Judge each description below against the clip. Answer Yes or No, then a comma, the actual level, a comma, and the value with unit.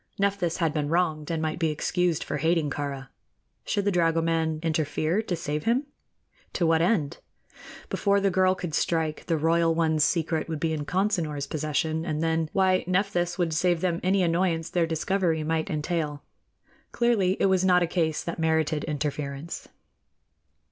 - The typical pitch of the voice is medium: Yes, medium, 165 Hz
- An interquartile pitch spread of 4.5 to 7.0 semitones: No, narrow, 2.5 semitones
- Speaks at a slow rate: No, average, 165 wpm